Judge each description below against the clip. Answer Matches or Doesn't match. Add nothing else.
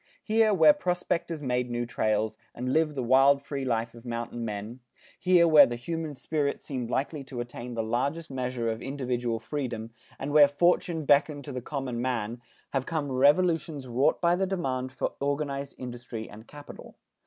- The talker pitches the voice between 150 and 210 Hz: Doesn't match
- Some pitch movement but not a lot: Matches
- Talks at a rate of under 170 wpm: Doesn't match